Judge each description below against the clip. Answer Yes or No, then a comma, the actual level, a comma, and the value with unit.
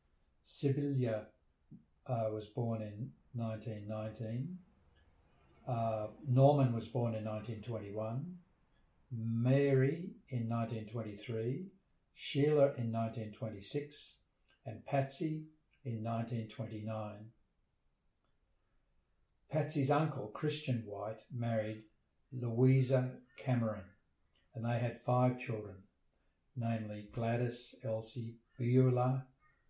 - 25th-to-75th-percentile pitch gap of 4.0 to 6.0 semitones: No, average, 3.3 semitones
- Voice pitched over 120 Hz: No, low, 115 Hz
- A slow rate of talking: Yes, slow, 75 wpm